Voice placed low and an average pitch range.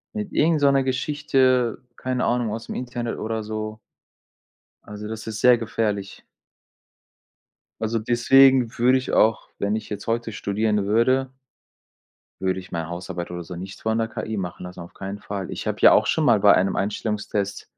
Yes: low, 110 Hz; average, 3.6 semitones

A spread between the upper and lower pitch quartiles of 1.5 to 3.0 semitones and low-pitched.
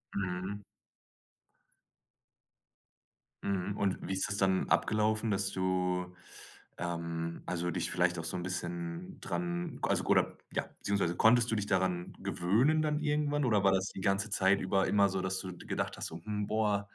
Yes: narrow, 2.5 semitones; very low, 95 Hz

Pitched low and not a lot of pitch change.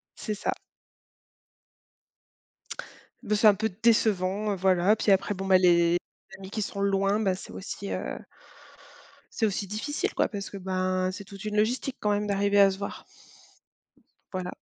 No: high, 200 Hz; narrow, 2.0 semitones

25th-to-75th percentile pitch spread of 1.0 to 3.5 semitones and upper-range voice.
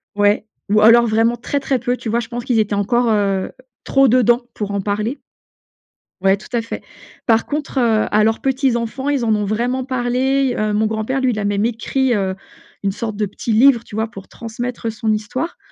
Yes: average, 2.9 semitones; high, 230 Hz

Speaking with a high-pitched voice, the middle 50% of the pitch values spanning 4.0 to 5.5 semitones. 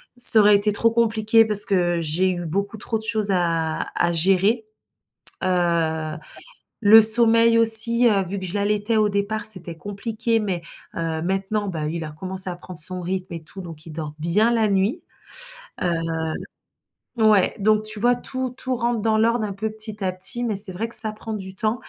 No: high, 205 Hz; average, 3.6 semitones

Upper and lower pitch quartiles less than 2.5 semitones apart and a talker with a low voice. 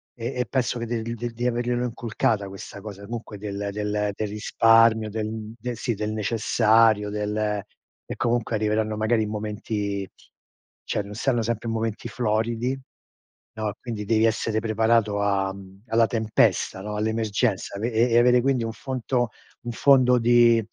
Yes: narrow, 2.0 semitones; low, 110 Hz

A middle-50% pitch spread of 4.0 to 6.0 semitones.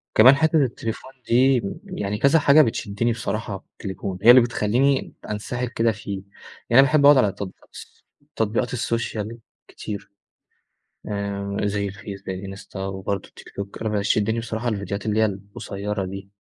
No: average, 3.3 semitones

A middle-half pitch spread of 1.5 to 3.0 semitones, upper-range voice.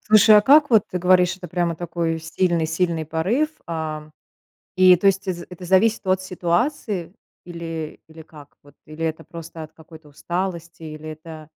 No: narrow, 2.6 semitones; medium, 170 Hz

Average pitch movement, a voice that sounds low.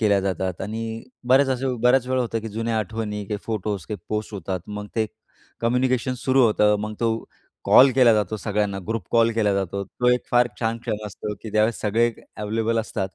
No: narrow, 2.1 semitones; low, 110 Hz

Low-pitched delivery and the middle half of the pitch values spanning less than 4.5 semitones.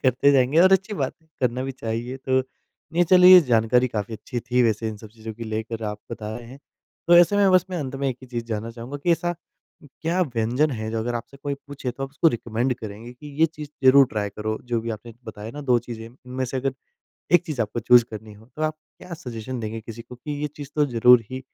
Yes: low, 125 Hz; average, 4.0 semitones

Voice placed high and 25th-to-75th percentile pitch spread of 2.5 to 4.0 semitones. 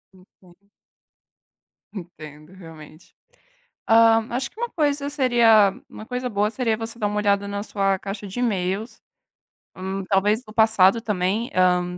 Yes: high, 205 Hz; average, 3.5 semitones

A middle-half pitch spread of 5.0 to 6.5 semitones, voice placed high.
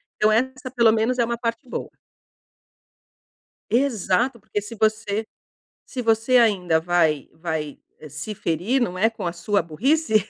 Yes: average, 5.3 semitones; high, 220 Hz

